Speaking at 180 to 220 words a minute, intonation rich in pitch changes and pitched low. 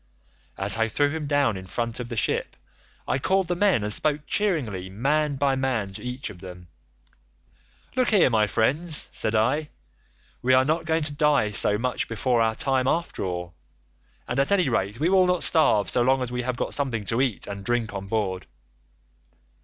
Yes: average, 195 wpm; wide, 5.7 semitones; low, 125 Hz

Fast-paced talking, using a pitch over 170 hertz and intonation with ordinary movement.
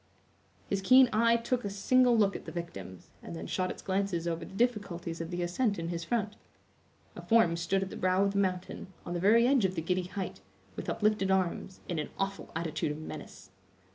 Yes: fast, 215 wpm; high, 190 Hz; average, 3.8 semitones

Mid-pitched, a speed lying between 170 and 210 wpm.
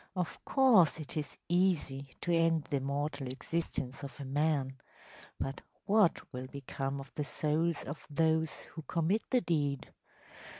No: medium, 150 Hz; average, 145 wpm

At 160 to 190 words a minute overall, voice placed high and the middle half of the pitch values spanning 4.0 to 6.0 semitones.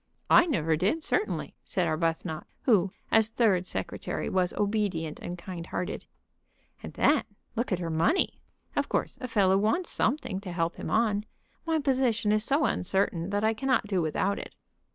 Yes: average, 170 wpm; high, 200 Hz; average, 4.6 semitones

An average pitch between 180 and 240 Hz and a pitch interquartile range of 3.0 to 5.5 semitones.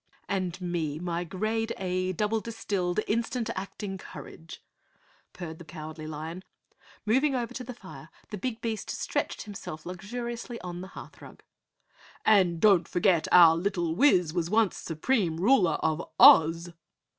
Yes: medium, 185 Hz; average, 4.5 semitones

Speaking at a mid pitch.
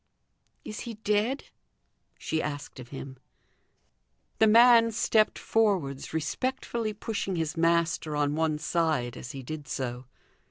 Yes: medium, 165 Hz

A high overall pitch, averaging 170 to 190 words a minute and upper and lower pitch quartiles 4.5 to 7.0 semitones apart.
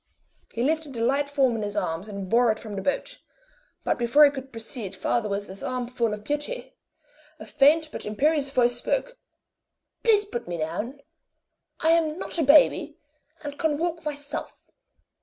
Yes: very high, 270 Hz; average, 175 wpm; wide, 5.4 semitones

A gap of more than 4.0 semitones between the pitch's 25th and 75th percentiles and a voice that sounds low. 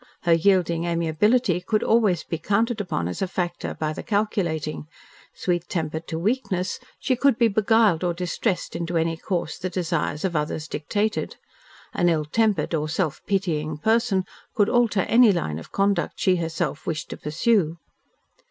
No: average, 4.5 semitones; medium, 175 Hz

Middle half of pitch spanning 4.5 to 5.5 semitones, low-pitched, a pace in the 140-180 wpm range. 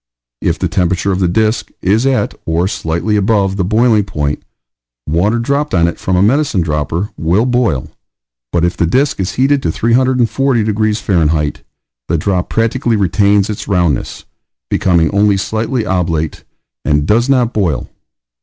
Yes: average, 5.1 semitones; low, 100 Hz; average, 155 wpm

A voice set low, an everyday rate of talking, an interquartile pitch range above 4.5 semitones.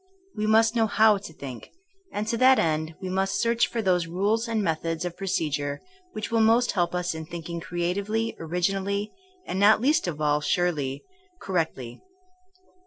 No: medium, 185 Hz; average, 170 wpm; average, 4.9 semitones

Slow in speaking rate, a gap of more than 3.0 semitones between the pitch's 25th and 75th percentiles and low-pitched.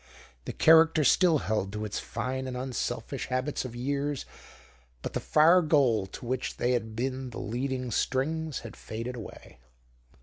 No: average, 160 wpm; average, 3.6 semitones; low, 130 Hz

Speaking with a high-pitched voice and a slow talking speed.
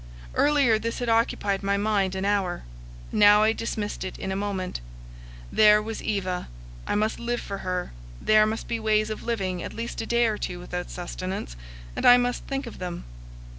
No: high, 210 Hz; average, 190 wpm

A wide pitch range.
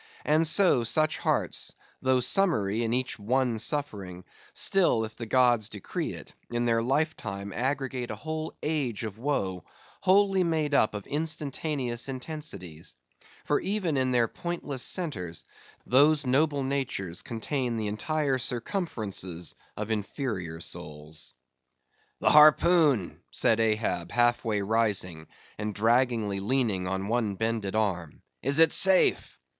Yes: wide, 6.0 semitones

